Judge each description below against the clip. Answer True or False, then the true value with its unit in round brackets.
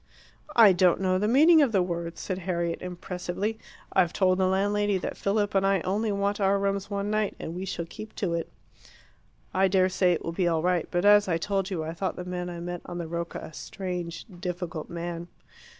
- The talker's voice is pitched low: False (185 Hz)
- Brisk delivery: True (215 wpm)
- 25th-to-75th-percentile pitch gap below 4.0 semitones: True (2.4 semitones)